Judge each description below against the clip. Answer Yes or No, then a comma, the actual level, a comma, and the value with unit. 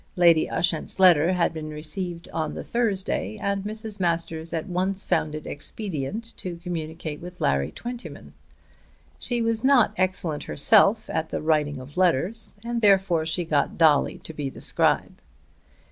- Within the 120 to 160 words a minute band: Yes, average, 155 wpm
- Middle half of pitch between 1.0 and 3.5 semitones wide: No, average, 4.2 semitones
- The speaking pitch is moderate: Yes, medium, 175 Hz